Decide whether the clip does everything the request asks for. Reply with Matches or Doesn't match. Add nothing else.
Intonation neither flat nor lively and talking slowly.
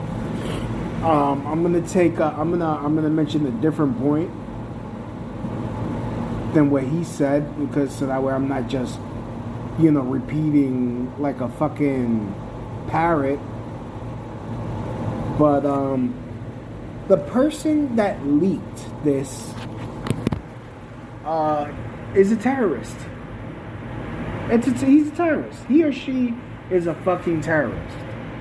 Matches